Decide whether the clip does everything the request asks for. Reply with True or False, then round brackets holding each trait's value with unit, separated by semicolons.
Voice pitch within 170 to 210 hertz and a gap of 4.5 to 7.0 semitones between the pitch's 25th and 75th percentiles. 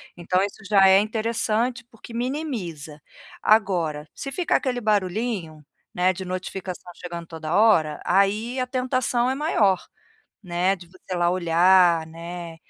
True (190 Hz; 4.9 semitones)